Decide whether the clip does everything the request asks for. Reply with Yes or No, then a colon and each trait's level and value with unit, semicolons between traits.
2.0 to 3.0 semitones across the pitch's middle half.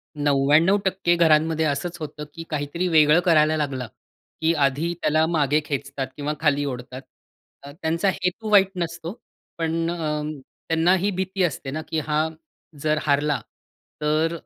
Yes: narrow, 2.5 semitones